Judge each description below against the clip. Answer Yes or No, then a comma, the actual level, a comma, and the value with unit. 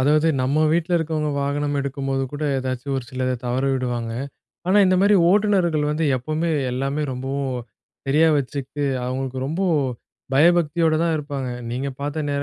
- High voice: No, medium, 145 Hz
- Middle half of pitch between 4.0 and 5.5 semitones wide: No, average, 3.3 semitones